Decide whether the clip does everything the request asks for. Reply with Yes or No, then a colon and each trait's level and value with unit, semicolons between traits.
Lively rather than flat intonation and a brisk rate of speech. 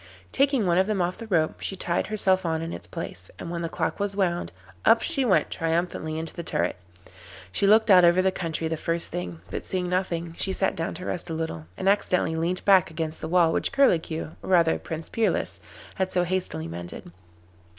No: average, 2.7 semitones; fast, 210 wpm